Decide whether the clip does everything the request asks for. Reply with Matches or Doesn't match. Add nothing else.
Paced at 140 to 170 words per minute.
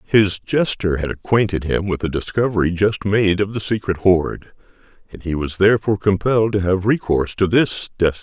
Doesn't match